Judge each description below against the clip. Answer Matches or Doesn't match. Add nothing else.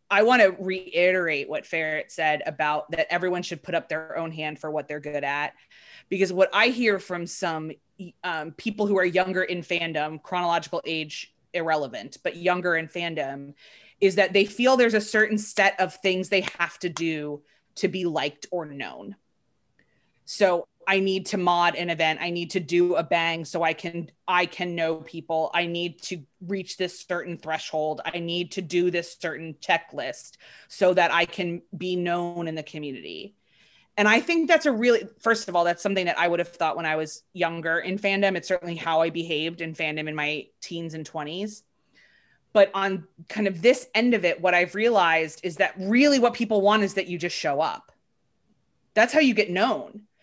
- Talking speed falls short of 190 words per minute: Doesn't match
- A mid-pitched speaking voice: Matches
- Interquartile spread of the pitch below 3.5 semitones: Matches